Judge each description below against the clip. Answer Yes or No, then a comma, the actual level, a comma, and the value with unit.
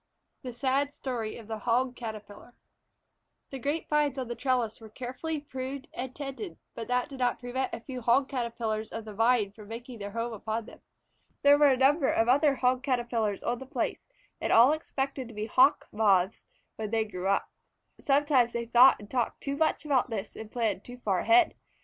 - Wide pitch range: No, average, 3.2 semitones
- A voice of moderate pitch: No, high, 245 Hz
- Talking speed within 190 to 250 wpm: Yes, average, 200 wpm